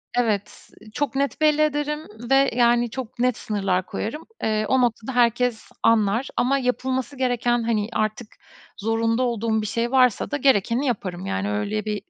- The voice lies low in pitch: No, high, 235 Hz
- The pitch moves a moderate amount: Yes, average, 3.4 semitones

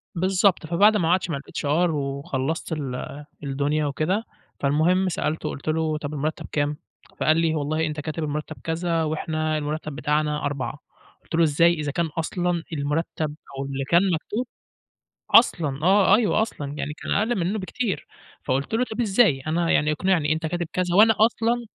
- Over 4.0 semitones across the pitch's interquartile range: No, average, 3.4 semitones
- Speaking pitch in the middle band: Yes, medium, 160 Hz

